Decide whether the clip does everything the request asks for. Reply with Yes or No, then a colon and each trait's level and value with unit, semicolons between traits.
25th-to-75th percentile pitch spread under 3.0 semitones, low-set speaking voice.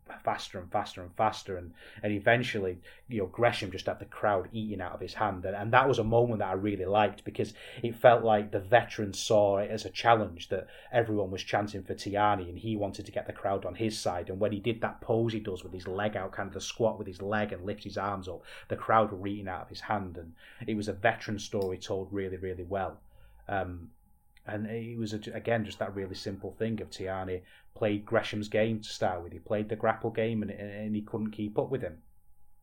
Yes: narrow, 2.6 semitones; low, 105 Hz